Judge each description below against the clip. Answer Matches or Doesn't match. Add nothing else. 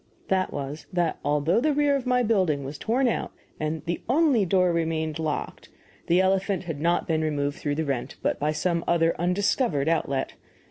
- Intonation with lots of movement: Doesn't match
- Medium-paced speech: Matches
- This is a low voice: Doesn't match